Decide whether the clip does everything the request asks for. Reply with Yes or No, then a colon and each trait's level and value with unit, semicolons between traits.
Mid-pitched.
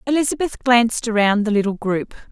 No: high, 230 Hz